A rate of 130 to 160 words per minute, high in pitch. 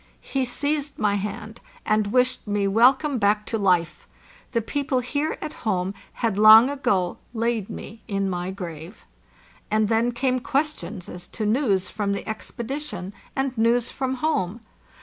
Yes: average, 150 wpm; high, 225 Hz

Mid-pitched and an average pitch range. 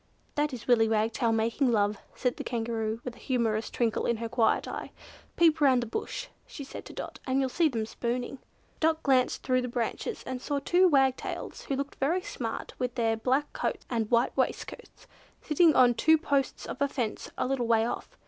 No: very high, 250 Hz; average, 3.4 semitones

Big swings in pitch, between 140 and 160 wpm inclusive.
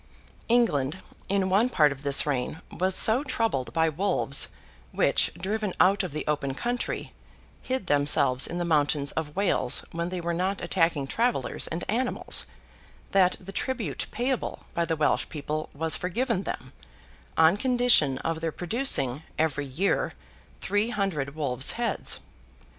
Yes: wide, 5.8 semitones; average, 145 wpm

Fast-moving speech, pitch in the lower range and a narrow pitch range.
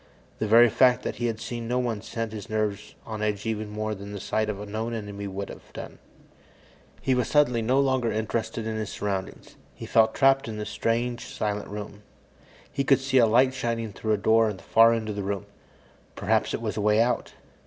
Yes: fast, 220 wpm; low, 110 Hz; narrow, 2.2 semitones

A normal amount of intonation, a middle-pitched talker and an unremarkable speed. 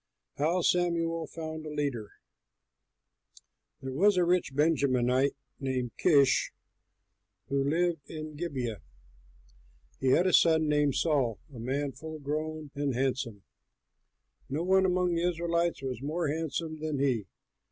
No: average, 3.8 semitones; medium, 150 Hz; slow, 130 wpm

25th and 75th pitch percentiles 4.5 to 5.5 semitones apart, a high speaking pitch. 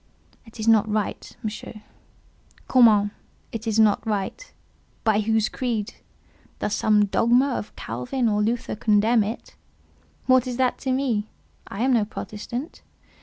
No: narrow, 2.6 semitones; high, 220 Hz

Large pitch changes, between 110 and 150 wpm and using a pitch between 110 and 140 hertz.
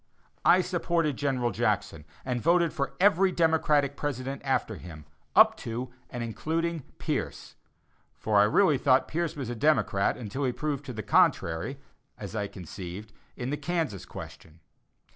Yes: wide, 6.3 semitones; average, 145 wpm; low, 135 Hz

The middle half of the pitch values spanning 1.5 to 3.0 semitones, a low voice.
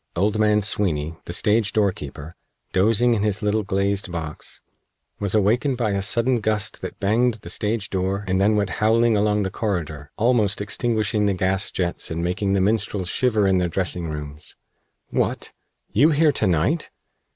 Yes: average, 2.7 semitones; low, 100 Hz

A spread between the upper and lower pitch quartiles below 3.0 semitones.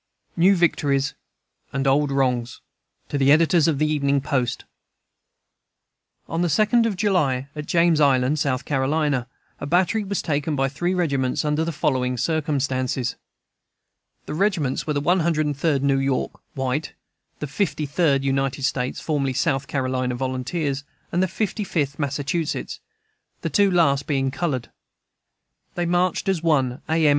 No: average, 3.7 semitones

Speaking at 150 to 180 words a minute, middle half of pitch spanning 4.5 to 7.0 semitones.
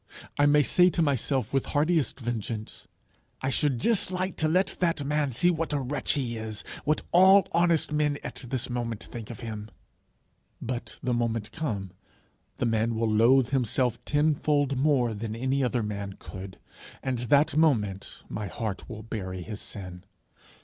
Yes: average, 165 wpm; average, 5.0 semitones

